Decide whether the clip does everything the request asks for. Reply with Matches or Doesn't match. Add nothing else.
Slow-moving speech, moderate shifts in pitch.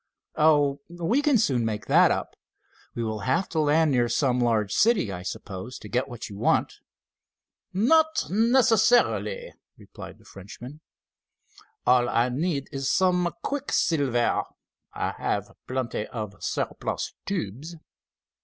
Doesn't match